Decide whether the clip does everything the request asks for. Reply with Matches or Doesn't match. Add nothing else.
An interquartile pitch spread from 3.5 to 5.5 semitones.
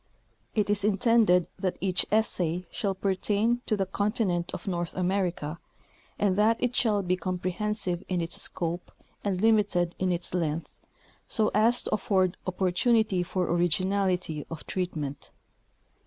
Doesn't match